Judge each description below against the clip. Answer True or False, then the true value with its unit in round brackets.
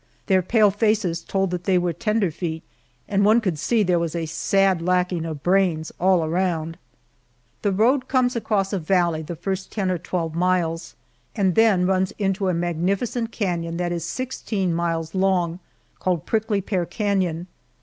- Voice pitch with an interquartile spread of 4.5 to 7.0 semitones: False (2.9 semitones)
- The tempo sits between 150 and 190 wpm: True (165 wpm)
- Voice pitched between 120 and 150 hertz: False (185 Hz)